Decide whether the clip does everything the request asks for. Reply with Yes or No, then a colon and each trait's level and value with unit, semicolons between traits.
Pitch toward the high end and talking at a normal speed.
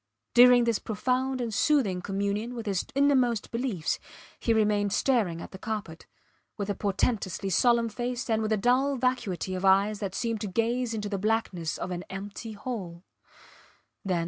Yes: high, 215 Hz; average, 165 wpm